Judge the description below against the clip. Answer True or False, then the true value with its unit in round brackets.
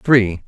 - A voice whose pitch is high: False (110 Hz)